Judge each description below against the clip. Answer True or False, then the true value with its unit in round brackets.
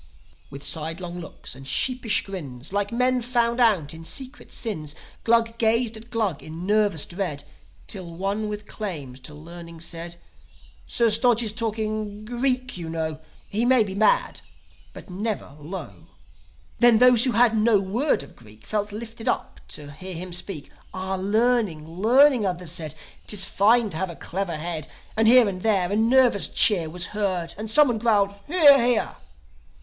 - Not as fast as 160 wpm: False (165 wpm)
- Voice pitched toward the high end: True (205 Hz)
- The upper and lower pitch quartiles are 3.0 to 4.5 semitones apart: False (5.3 semitones)